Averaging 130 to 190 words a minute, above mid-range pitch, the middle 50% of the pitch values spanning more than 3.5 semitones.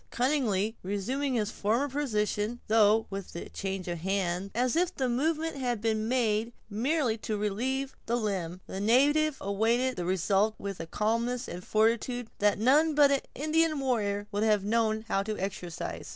Yes: average, 165 wpm; high, 220 Hz; average, 4.3 semitones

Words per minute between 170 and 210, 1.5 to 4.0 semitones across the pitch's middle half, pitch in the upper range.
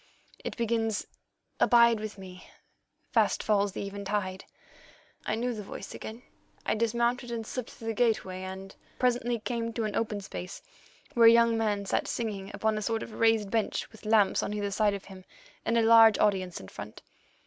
Yes: average, 180 wpm; narrow, 2.4 semitones; high, 220 Hz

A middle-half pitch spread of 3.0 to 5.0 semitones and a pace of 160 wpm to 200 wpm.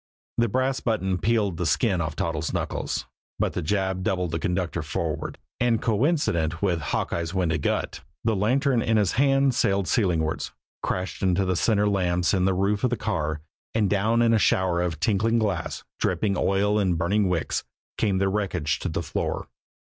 Yes: average, 4.0 semitones; average, 180 wpm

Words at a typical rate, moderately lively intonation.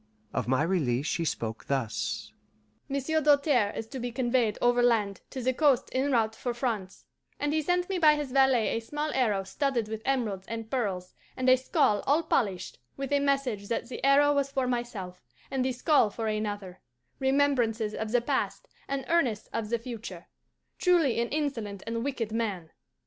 Yes: average, 180 wpm; average, 4.7 semitones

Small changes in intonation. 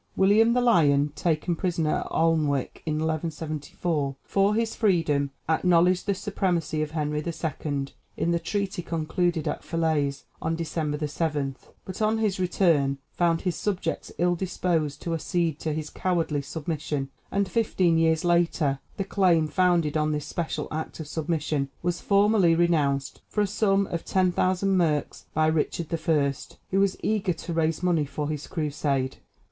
No: average, 3.2 semitones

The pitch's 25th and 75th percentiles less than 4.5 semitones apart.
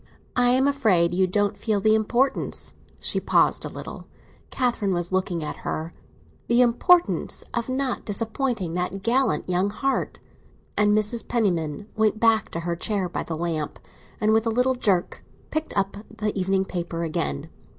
No: average, 4.9 semitones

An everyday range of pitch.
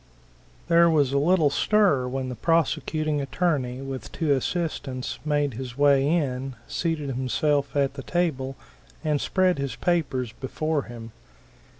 Yes: average, 3.5 semitones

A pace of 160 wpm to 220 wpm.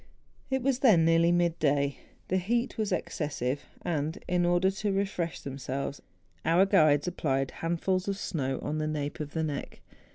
Yes: average, 170 wpm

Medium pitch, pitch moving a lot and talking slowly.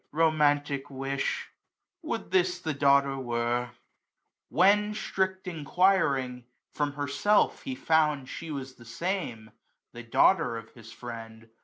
Yes: medium, 145 Hz; wide, 6.4 semitones; slow, 130 wpm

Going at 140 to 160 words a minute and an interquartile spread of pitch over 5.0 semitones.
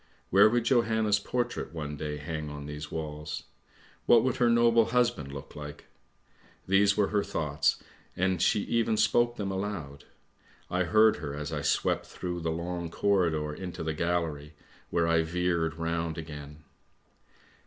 Yes: average, 155 wpm; wide, 5.5 semitones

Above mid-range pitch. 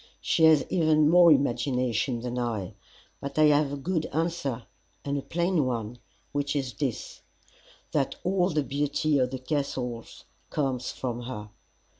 No: medium, 140 Hz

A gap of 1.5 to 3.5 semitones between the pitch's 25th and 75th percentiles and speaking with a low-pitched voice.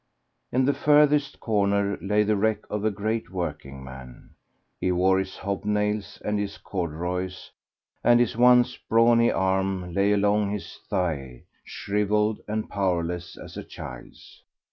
Yes: average, 2.8 semitones; low, 100 Hz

